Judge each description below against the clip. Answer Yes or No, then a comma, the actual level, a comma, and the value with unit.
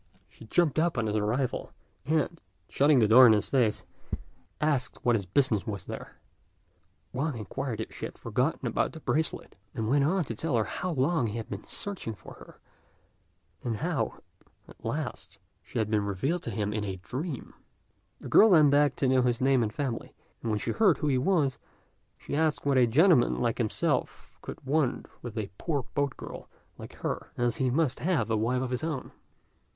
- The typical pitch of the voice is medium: No, low, 130 Hz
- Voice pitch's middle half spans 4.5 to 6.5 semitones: Yes, average, 5.2 semitones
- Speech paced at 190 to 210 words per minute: Yes, average, 195 wpm